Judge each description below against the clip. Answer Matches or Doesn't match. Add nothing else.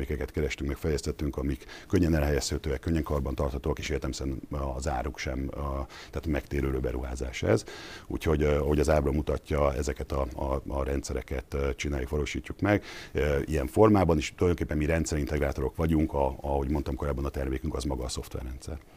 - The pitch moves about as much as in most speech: Doesn't match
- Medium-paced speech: Doesn't match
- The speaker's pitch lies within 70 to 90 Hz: Matches